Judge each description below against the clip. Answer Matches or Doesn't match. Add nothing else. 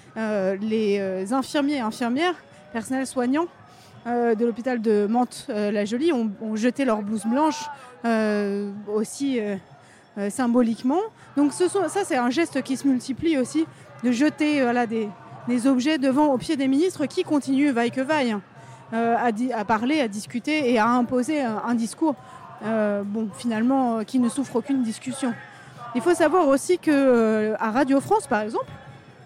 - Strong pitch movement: Doesn't match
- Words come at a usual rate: Matches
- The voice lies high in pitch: Matches